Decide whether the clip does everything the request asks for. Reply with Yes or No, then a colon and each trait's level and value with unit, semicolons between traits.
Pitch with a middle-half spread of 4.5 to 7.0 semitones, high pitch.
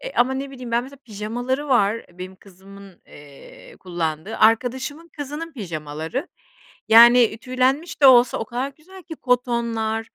Yes: average, 4.9 semitones; high, 240 Hz